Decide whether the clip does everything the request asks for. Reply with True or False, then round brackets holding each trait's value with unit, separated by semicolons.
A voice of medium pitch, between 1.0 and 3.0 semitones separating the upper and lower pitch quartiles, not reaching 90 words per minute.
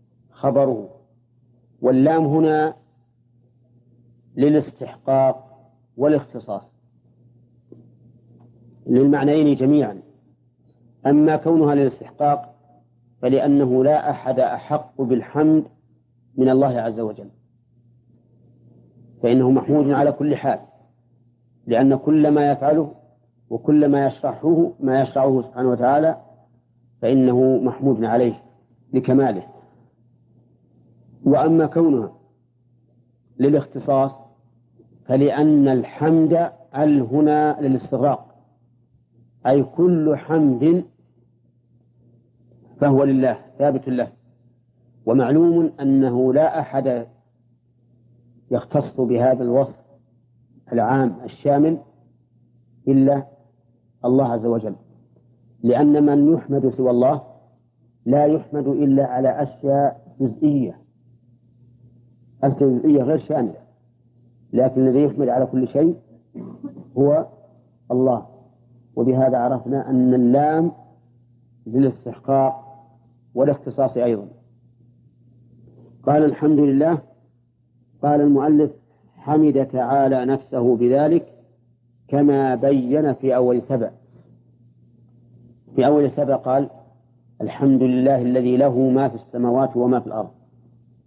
False (125 Hz; 2.5 semitones; 80 wpm)